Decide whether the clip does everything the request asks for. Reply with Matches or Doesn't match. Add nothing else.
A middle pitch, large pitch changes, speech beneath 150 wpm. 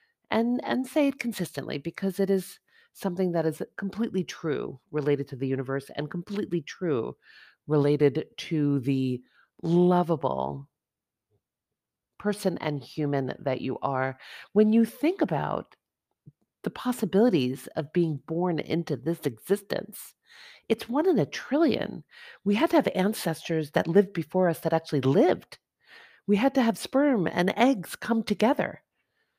Matches